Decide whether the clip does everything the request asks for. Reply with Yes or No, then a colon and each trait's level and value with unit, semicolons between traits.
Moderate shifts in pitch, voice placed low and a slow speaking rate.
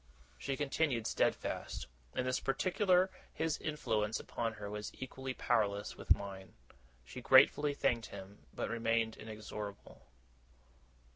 Yes: average, 4.6 semitones; low, 115 Hz; slow, 120 wpm